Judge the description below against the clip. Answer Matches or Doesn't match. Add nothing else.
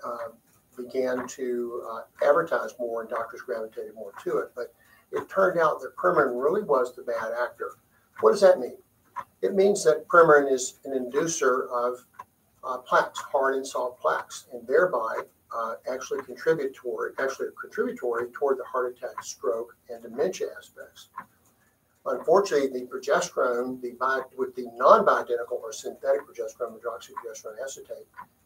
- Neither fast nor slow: Matches